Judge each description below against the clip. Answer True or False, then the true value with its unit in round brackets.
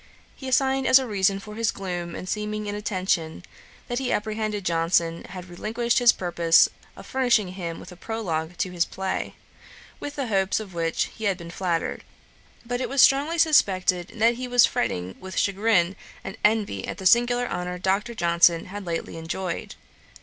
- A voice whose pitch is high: True (195 Hz)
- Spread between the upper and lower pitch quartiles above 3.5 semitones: True (4.7 semitones)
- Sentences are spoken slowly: False (175 wpm)